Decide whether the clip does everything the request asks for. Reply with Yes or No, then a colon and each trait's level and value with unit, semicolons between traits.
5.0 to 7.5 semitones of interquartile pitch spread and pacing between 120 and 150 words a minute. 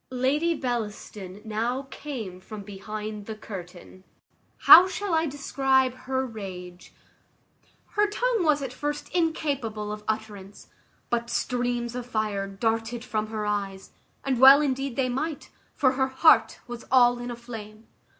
No: average, 4.1 semitones; average, 140 wpm